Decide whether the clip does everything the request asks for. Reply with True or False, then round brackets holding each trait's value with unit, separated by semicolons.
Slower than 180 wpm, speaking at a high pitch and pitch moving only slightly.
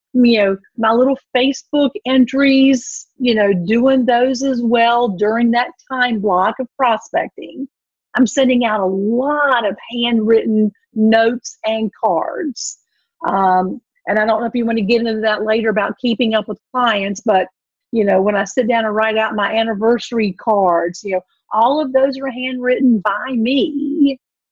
False (165 wpm; 235 Hz; 3.2 semitones)